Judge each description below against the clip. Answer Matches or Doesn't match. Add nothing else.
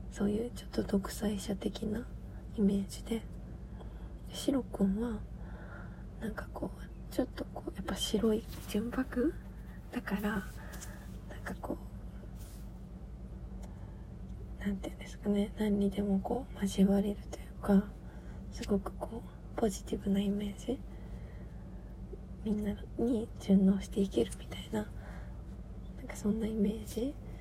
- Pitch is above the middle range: Matches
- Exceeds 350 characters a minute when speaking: Doesn't match